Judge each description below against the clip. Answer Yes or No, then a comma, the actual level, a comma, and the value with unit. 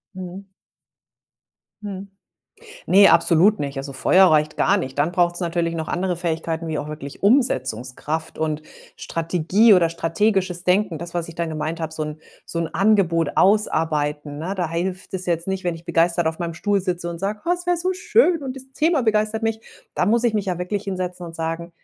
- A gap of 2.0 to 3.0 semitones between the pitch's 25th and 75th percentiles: No, average, 3.5 semitones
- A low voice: No, medium, 175 Hz